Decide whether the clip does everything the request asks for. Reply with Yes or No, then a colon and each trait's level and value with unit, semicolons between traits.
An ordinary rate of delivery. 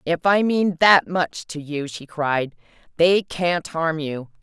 Yes: average, 175 wpm